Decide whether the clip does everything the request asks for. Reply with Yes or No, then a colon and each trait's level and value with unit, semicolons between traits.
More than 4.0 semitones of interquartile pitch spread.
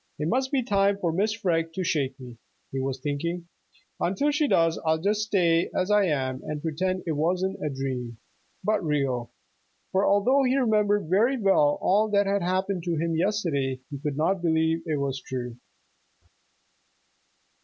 Yes: wide, 5.5 semitones